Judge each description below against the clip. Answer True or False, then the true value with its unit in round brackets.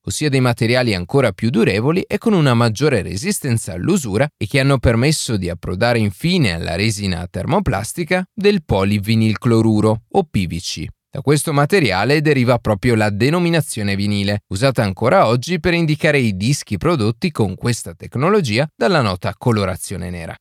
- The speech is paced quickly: False (145 wpm)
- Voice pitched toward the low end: True (120 Hz)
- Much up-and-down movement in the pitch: True (6.3 semitones)